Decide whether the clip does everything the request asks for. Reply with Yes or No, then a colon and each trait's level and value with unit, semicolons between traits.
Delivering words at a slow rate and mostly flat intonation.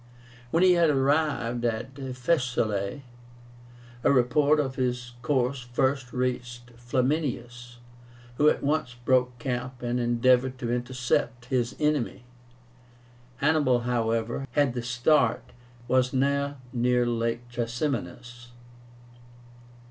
Yes: slow, 110 wpm; narrow, 2.1 semitones